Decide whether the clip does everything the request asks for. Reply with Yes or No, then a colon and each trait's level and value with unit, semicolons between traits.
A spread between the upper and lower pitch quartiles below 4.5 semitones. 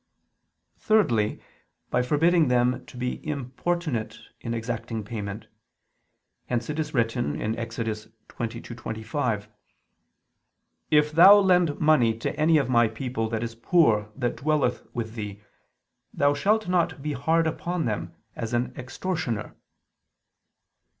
No: average, 5.3 semitones